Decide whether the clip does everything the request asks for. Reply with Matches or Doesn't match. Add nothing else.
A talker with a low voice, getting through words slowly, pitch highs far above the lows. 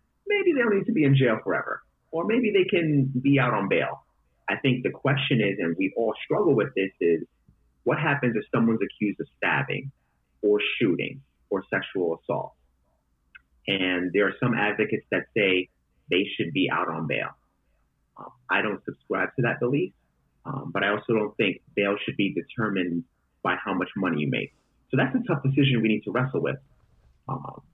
Doesn't match